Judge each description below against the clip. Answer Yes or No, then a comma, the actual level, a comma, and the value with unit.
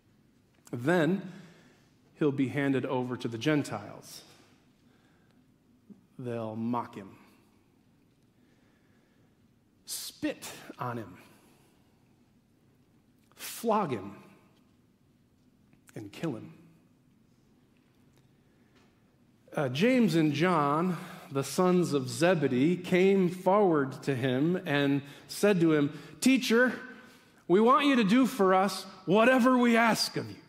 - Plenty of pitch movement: Yes, wide, 6.2 semitones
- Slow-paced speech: Yes, slow, 95 wpm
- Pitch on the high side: No, medium, 170 Hz